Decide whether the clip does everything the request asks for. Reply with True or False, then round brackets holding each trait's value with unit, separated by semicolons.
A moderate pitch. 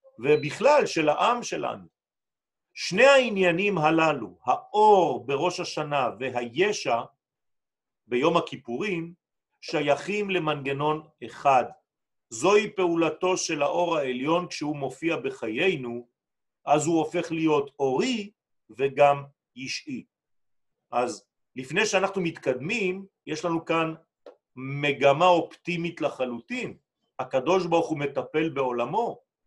True (165 Hz)